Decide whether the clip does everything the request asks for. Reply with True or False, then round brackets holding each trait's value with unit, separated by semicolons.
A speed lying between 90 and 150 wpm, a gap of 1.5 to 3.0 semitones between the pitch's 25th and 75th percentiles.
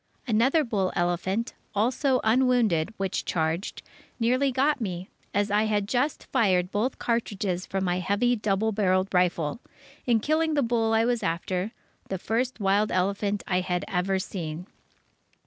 False (145 wpm; 4.4 semitones)